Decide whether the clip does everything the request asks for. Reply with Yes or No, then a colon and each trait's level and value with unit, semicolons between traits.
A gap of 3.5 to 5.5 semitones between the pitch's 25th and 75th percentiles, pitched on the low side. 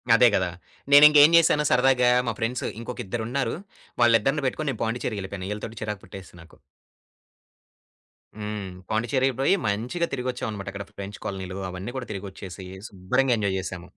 Yes: average, 4.5 semitones; low, 110 Hz